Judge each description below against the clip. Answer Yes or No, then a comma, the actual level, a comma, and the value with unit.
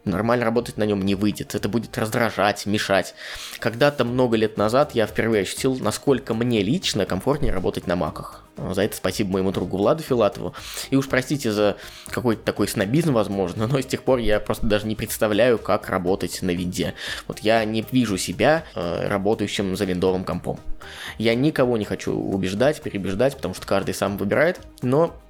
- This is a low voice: Yes, low, 105 Hz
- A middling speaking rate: No, fast, 175 wpm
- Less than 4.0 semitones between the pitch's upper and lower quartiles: Yes, average, 3.6 semitones